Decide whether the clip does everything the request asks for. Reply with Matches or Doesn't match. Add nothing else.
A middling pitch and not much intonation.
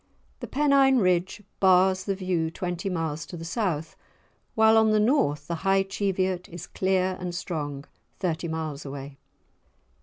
Doesn't match